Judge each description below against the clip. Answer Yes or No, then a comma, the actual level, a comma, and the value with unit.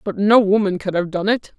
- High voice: Yes, high, 200 Hz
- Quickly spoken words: Yes, fast, 265 wpm